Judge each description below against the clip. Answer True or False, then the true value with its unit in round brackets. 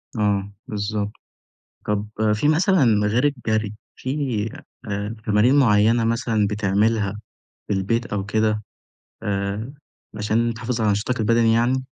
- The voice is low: True (110 Hz)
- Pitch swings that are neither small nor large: False (2.1 semitones)